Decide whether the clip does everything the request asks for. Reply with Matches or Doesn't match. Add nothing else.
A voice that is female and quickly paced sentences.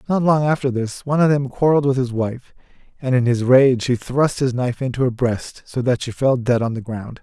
Doesn't match